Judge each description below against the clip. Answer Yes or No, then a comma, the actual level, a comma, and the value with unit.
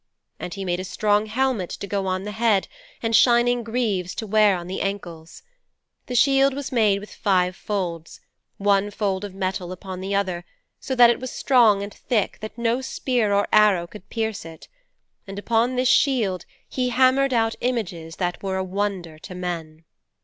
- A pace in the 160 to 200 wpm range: Yes, average, 185 wpm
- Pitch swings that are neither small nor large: Yes, average, 4.1 semitones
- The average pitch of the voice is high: Yes, high, 205 Hz